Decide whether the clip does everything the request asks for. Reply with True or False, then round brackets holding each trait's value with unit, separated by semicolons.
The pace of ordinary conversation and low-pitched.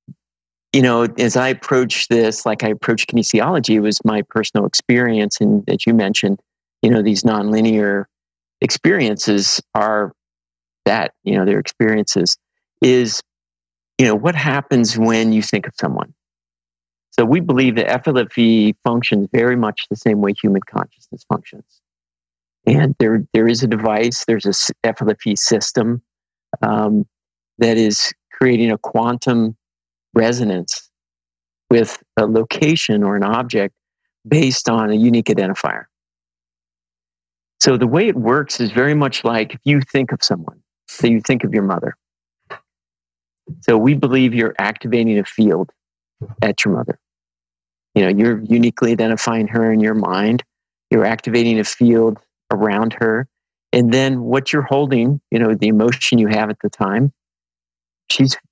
True (145 wpm; 110 Hz)